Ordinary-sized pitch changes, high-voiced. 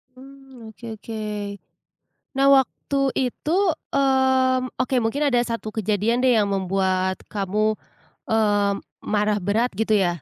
Yes: average, 4.1 semitones; high, 220 Hz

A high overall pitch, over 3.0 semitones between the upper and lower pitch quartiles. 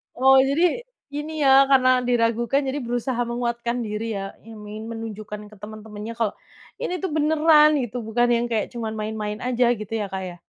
Yes: high, 235 Hz; average, 3.6 semitones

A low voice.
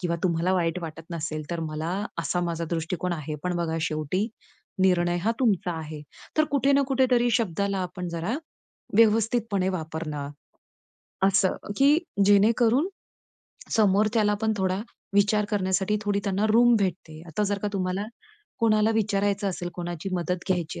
No: high, 190 Hz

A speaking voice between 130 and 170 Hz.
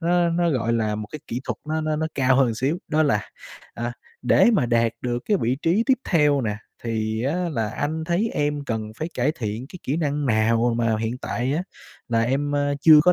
Yes: low, 135 Hz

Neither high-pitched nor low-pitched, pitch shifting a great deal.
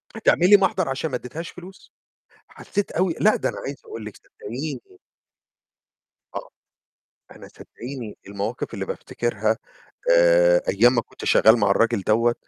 No: low, 130 Hz; wide, 8.6 semitones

